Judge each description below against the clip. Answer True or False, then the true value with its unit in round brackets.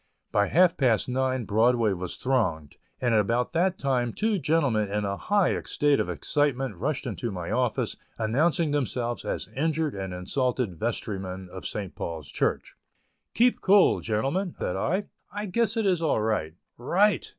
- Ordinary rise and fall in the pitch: False (7.7 semitones)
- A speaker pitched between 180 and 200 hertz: False (125 Hz)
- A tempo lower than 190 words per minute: True (160 wpm)